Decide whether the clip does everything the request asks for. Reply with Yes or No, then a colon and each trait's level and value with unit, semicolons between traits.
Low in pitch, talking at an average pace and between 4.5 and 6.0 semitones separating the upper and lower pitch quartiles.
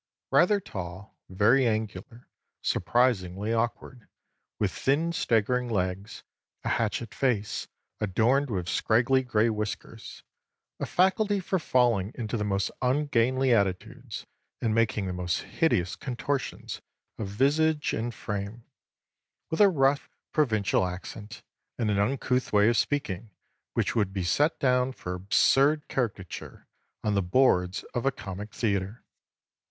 No: low, 115 Hz; slow, 125 wpm; average, 4.8 semitones